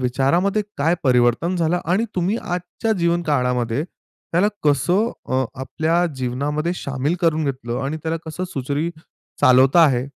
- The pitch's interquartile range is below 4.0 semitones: No, average, 4.8 semitones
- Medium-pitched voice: Yes, medium, 155 Hz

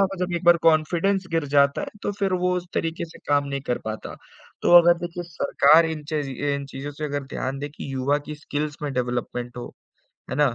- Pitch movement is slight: No, average, 3.5 semitones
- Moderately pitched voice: Yes, medium, 150 Hz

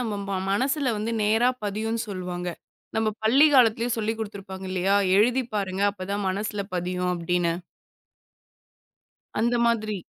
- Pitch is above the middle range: Yes, high, 210 Hz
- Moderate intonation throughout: Yes, average, 3.3 semitones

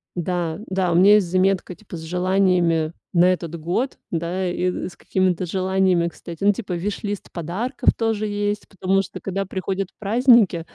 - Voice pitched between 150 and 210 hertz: Yes, medium, 185 Hz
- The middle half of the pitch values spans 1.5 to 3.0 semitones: Yes, narrow, 2.5 semitones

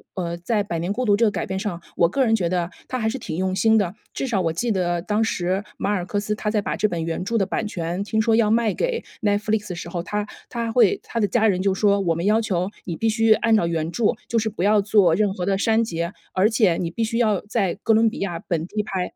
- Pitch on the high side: Yes, high, 205 Hz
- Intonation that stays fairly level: No, average, 3.7 semitones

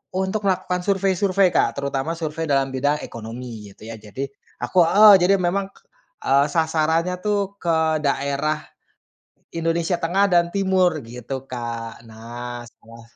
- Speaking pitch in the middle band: Yes, medium, 155 Hz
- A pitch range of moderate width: No, wide, 6.9 semitones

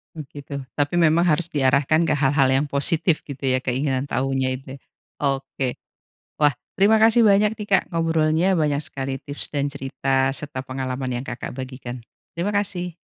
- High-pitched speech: No, medium, 145 Hz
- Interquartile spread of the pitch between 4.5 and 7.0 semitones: No, average, 3.8 semitones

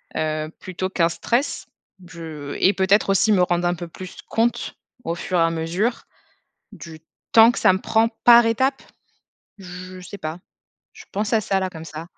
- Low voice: No, medium, 185 Hz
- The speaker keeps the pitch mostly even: No, average, 4.4 semitones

